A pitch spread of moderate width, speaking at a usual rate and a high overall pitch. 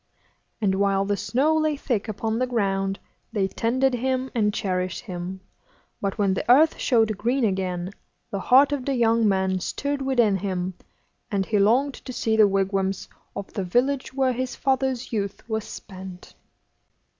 Yes: average, 4.8 semitones; average, 165 wpm; high, 220 Hz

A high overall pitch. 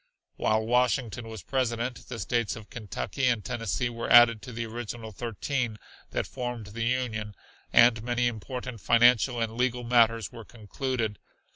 No: low, 115 Hz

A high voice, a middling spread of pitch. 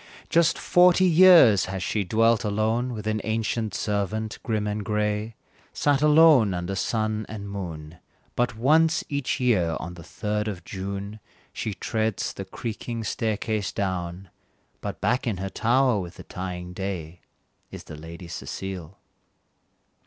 No: low, 105 Hz; average, 3.4 semitones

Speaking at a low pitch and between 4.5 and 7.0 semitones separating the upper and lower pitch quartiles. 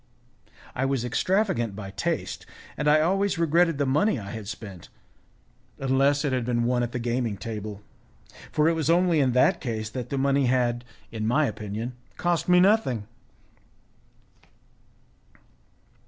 Yes: low, 130 Hz; average, 5.3 semitones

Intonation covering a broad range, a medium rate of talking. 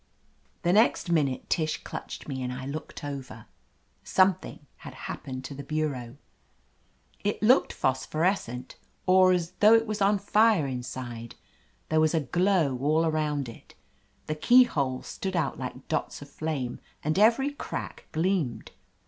Yes: wide, 6.2 semitones; average, 145 wpm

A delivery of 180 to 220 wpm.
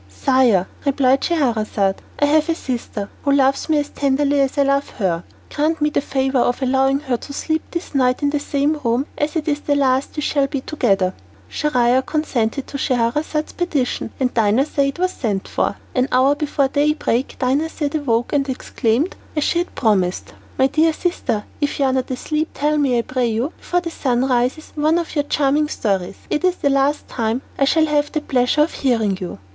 Yes: average, 200 wpm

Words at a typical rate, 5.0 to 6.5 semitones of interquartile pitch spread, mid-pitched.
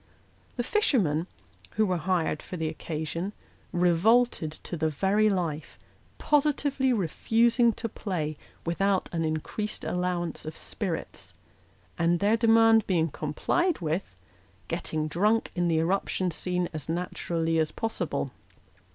No: slow, 125 wpm; wide, 5.4 semitones; medium, 180 Hz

